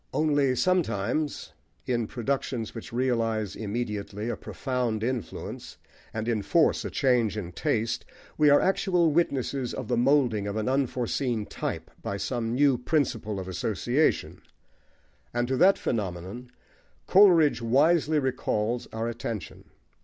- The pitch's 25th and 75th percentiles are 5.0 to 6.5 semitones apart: No, average, 4.4 semitones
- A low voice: Yes, low, 120 Hz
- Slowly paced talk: Yes, slow, 125 wpm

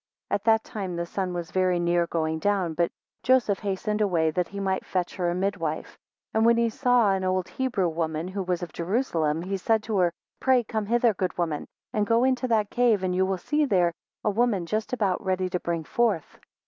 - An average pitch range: Yes, average, 4.0 semitones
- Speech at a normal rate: No, fast, 220 wpm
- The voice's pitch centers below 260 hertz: Yes, high, 190 Hz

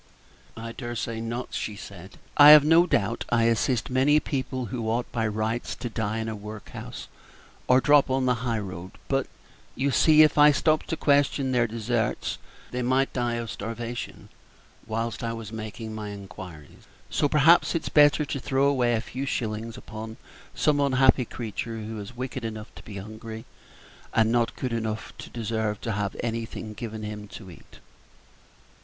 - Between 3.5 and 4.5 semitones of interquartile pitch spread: No, average, 3.1 semitones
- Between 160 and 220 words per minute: Yes, average, 175 wpm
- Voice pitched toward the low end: Yes, low, 115 Hz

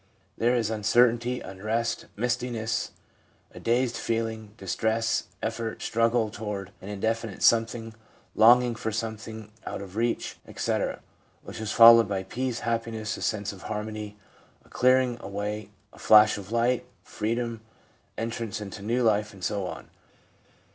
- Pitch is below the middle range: Yes, low, 110 Hz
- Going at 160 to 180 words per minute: No, slow, 135 wpm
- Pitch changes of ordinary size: No, narrow, 1.8 semitones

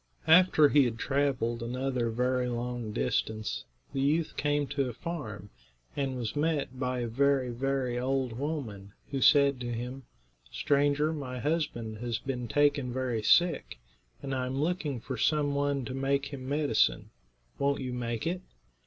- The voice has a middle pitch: No, low, 130 Hz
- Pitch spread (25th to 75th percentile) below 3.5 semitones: Yes, average, 2.9 semitones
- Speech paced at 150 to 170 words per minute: Yes, average, 160 wpm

